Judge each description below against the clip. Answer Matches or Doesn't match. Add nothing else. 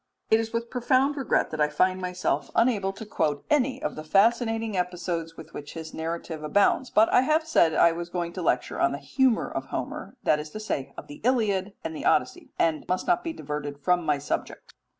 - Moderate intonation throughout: Doesn't match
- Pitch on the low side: Doesn't match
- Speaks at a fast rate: Matches